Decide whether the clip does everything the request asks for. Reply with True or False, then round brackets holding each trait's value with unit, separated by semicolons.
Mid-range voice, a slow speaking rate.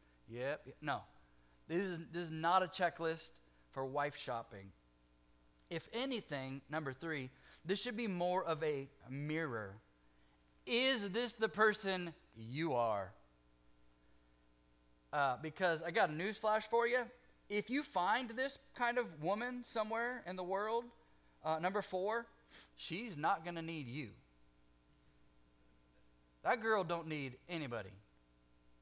True (155 Hz; 130 wpm)